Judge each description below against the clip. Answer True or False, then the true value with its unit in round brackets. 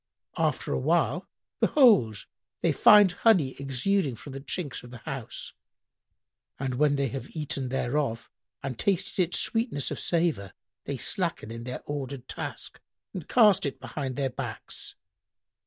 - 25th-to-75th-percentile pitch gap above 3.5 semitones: True (5.6 semitones)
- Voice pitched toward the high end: False (140 Hz)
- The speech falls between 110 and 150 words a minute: True (140 wpm)